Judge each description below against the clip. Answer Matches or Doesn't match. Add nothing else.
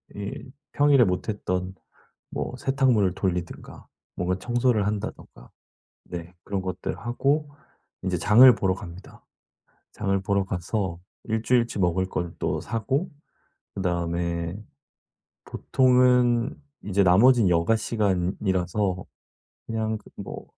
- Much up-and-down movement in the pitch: Doesn't match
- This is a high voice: Doesn't match